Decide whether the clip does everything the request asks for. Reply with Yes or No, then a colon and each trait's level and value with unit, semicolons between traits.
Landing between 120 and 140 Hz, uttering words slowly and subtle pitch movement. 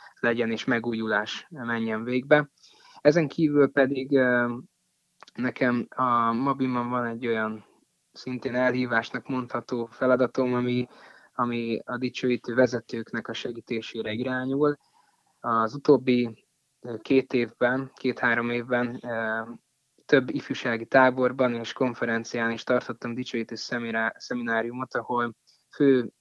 Yes: low, 125 Hz; slow, 100 wpm; narrow, 1.9 semitones